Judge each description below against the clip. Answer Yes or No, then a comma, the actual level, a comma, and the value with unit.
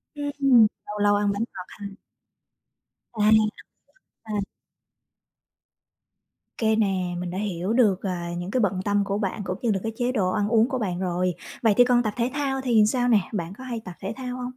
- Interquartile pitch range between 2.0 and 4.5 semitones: Yes, average, 4.2 semitones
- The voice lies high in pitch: Yes, high, 210 Hz